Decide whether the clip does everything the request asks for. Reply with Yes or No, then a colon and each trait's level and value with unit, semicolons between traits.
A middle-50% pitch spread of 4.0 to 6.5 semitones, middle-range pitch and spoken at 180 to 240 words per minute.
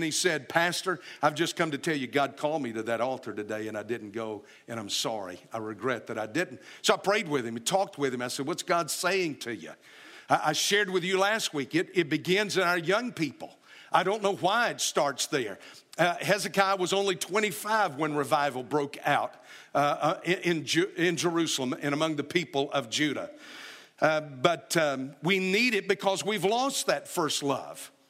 Yes: wide, 5.6 semitones; medium, 165 Hz; average, 190 wpm